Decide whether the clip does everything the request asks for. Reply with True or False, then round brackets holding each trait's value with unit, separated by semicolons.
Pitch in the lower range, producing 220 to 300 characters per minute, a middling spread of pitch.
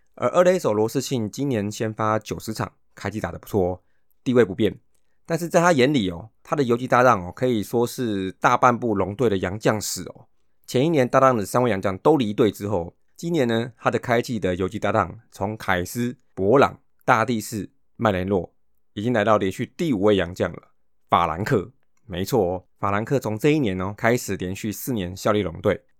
True (110 Hz; 295 characters per minute; 4.2 semitones)